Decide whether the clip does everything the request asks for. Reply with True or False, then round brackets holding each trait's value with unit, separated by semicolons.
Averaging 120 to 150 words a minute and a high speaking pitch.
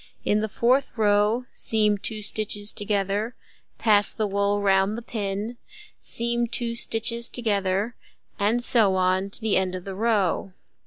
True (145 wpm; 210 Hz)